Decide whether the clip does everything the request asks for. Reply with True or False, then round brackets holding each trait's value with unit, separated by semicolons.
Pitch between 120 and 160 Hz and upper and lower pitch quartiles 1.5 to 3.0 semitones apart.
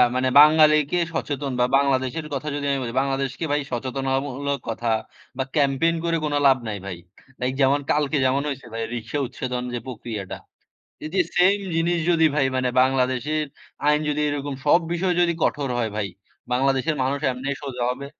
True (135 Hz; 2.7 semitones)